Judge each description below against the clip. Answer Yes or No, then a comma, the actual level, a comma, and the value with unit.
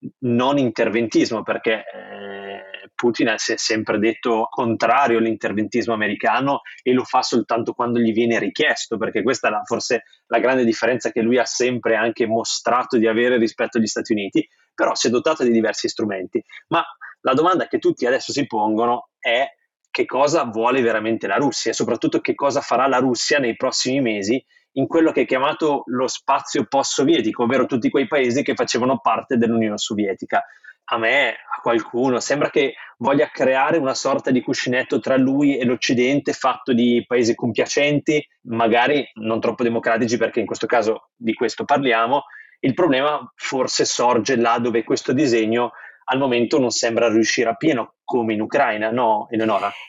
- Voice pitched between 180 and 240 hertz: No, low, 120 Hz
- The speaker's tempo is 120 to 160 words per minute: No, fast, 170 wpm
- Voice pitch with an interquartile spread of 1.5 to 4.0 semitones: Yes, average, 3.1 semitones